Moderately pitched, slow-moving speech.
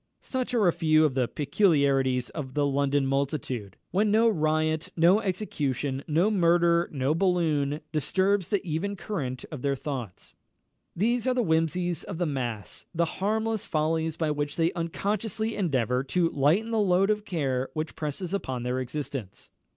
No: medium, 160 Hz; average, 160 wpm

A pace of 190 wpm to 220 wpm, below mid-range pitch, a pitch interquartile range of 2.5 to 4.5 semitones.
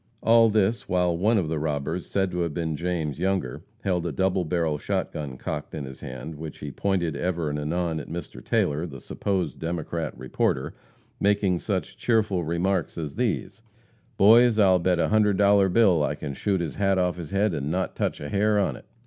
Yes: average, 200 wpm; very low, 90 Hz; average, 3.9 semitones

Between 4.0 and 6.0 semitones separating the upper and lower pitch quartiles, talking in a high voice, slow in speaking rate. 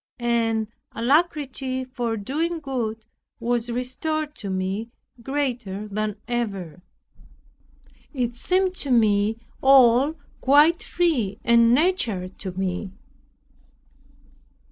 Yes: average, 4.5 semitones; high, 240 Hz; slow, 95 wpm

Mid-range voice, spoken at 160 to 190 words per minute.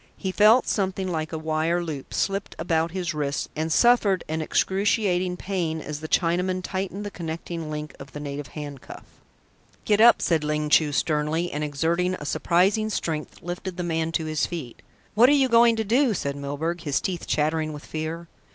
Yes: medium, 165 Hz; average, 185 wpm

